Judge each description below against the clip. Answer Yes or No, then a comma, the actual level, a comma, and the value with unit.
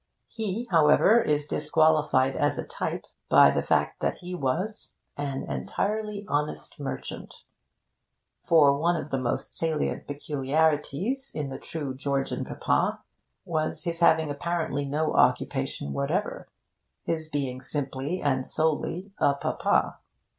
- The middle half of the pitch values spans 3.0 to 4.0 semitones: Yes, average, 3.3 semitones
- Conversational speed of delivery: No, slow, 125 wpm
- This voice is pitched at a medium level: Yes, medium, 150 Hz